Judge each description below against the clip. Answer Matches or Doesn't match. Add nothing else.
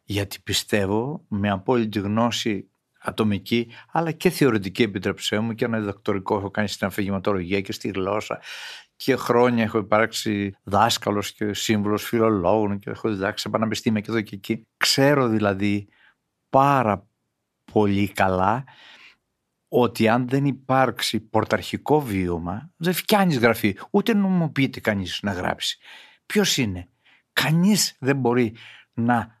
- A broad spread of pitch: Doesn't match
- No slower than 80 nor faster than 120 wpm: Doesn't match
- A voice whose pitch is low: Matches